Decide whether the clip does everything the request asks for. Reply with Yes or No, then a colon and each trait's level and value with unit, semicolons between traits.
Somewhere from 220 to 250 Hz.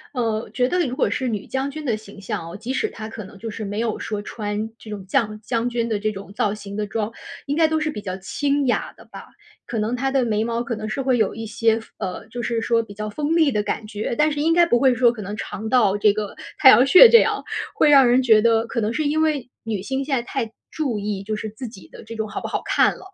Yes: high, 230 Hz